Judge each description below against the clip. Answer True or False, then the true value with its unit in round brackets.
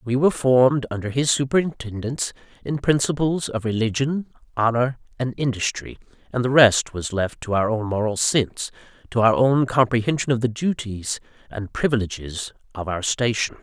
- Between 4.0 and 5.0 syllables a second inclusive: False (5.2 syllables/s)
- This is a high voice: False (120 Hz)